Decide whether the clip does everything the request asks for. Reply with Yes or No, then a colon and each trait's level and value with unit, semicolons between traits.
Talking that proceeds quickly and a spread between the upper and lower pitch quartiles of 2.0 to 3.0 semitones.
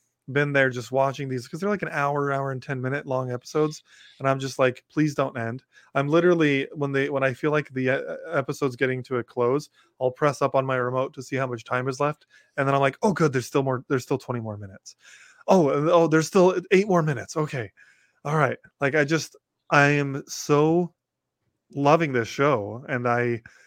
Yes: fast, 215 wpm; average, 2.7 semitones